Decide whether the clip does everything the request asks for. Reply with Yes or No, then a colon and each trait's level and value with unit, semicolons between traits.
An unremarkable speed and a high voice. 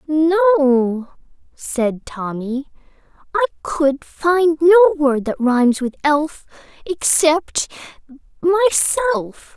No: slow, 90 wpm; very high, 305 Hz